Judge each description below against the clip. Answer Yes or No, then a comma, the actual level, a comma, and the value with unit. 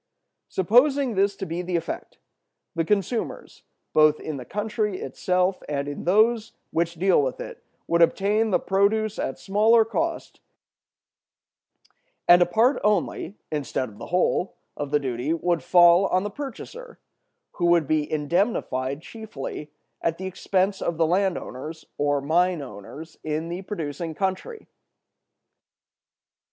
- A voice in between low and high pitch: Yes, medium, 175 Hz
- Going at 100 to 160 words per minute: Yes, average, 140 wpm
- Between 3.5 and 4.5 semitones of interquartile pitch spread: No, average, 4.9 semitones